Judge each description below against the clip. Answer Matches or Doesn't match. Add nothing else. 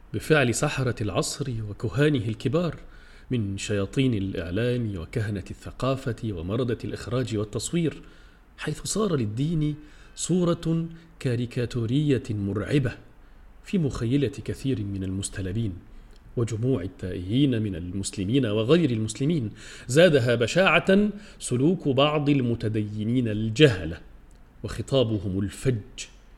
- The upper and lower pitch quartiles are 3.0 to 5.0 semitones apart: Doesn't match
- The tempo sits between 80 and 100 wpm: Matches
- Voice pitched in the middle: Doesn't match